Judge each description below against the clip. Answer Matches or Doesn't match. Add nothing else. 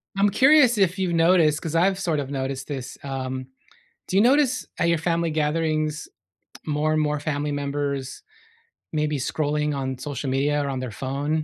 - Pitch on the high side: Doesn't match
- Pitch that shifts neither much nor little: Matches